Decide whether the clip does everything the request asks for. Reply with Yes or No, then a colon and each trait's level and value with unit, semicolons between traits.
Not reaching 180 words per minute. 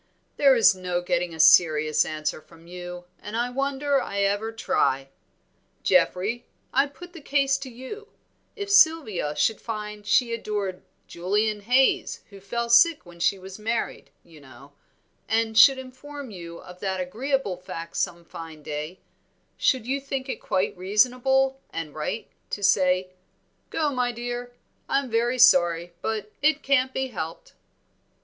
Yes: average, 150 wpm